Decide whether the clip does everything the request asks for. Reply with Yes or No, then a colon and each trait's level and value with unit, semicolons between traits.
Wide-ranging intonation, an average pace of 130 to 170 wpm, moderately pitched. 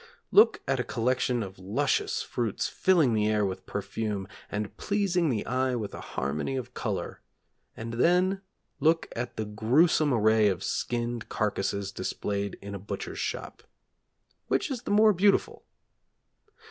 No: wide, 7.6 semitones; average, 145 wpm; low, 115 Hz